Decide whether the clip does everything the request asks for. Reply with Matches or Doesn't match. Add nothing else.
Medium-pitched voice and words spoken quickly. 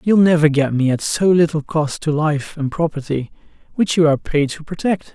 Matches